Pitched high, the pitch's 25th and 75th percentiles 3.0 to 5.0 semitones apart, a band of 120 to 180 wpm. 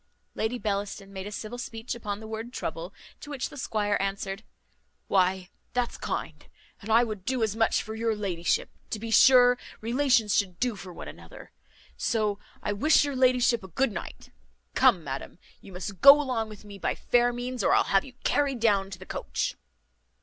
No: high, 220 Hz; average, 3.7 semitones; average, 190 wpm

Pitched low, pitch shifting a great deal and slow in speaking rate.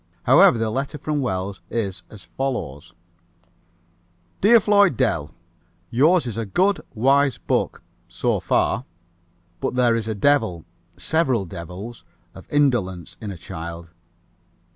Yes: low, 115 Hz; wide, 7.2 semitones; slow, 125 wpm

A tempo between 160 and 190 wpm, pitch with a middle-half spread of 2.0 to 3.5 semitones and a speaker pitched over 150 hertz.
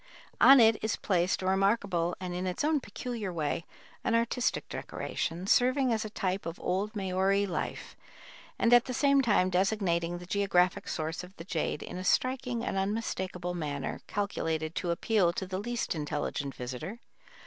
No: average, 170 wpm; average, 4.2 semitones; high, 190 Hz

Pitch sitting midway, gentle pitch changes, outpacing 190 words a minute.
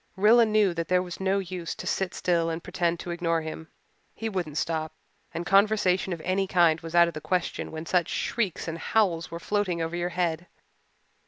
Yes: medium, 175 Hz; narrow, 2.3 semitones; average, 200 wpm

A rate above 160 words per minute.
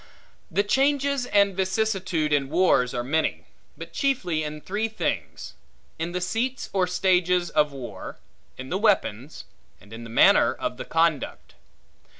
No: average, 155 wpm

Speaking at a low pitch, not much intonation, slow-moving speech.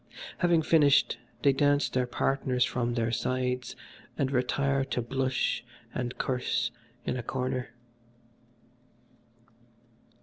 Yes: low, 130 Hz; narrow, 1.7 semitones; slow, 105 wpm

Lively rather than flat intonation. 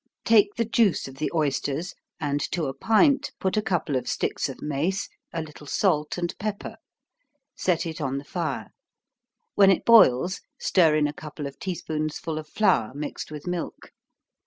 No: average, 4.5 semitones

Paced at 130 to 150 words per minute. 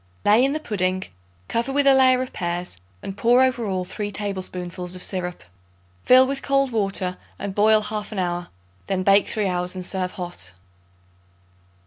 No: average, 170 wpm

